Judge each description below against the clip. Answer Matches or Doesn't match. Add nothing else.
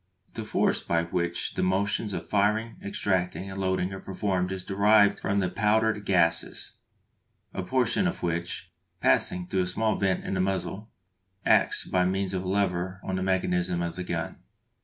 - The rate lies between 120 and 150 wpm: Doesn't match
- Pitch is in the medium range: Doesn't match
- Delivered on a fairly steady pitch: Matches